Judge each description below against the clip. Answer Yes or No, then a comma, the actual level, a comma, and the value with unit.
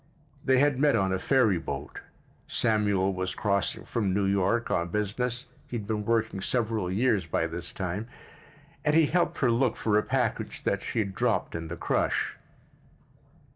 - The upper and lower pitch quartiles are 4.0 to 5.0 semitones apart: Yes, average, 4.3 semitones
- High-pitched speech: No, low, 105 Hz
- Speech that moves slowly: No, average, 175 wpm